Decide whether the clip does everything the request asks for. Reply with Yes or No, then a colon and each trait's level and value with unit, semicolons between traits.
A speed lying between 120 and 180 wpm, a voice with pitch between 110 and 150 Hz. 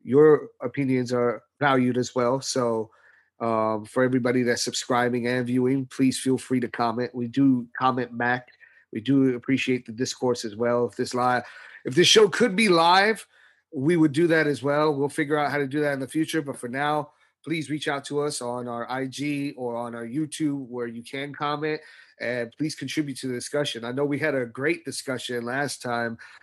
No: average, 200 wpm; low, 130 Hz